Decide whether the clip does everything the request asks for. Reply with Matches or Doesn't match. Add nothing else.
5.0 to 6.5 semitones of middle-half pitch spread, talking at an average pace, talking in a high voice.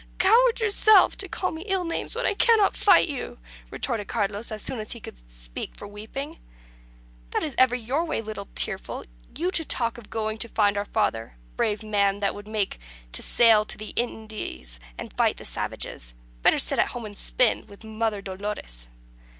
Matches